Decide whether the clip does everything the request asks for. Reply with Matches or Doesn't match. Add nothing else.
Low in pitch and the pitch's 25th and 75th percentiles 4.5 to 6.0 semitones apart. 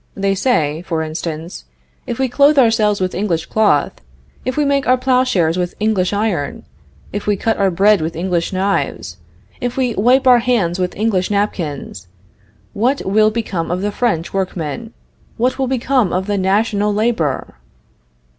Doesn't match